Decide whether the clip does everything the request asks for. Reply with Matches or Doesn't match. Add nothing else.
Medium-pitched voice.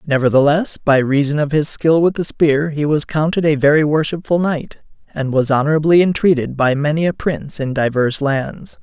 Matches